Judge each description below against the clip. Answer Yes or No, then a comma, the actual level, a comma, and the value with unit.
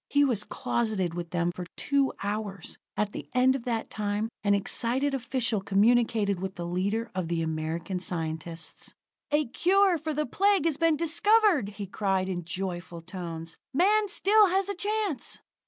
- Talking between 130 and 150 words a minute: No, average, 165 wpm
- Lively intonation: Yes, wide, 8.6 semitones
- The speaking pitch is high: Yes, high, 215 Hz